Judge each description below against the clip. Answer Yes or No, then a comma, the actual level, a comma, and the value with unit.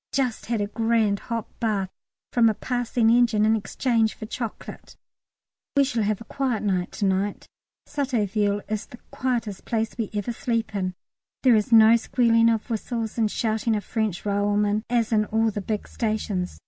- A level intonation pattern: Yes, narrow, 2.1 semitones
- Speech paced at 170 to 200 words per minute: Yes, average, 175 wpm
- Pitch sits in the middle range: No, high, 220 Hz